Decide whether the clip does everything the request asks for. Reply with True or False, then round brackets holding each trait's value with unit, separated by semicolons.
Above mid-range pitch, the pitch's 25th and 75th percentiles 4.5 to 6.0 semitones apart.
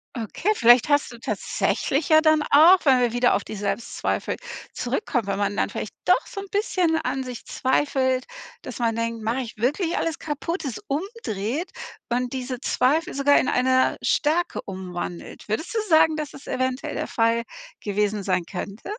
True (255 Hz; 5.4 semitones)